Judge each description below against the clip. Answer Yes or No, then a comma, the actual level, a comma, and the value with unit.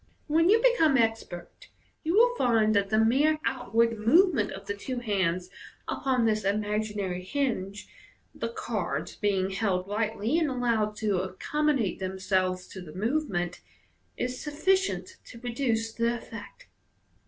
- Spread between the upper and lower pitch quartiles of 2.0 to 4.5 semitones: No, average, 5.1 semitones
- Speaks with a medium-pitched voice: No, high, 225 Hz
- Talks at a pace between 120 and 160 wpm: Yes, slow, 135 wpm